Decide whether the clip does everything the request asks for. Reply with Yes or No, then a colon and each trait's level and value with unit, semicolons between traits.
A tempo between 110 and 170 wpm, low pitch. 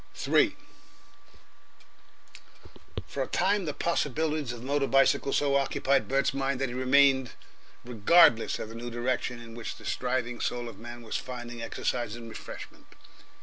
Yes: average, 150 wpm; low, 125 Hz